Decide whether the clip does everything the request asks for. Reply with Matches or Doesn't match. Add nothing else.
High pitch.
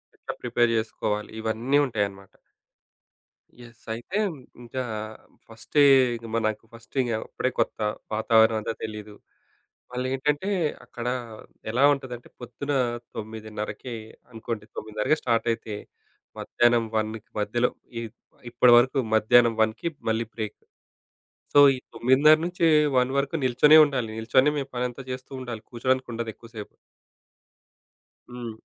Doesn't match